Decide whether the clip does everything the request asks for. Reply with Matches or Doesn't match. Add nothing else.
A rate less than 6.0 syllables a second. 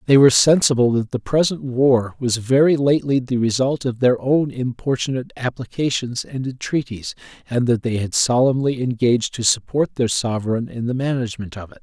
Matches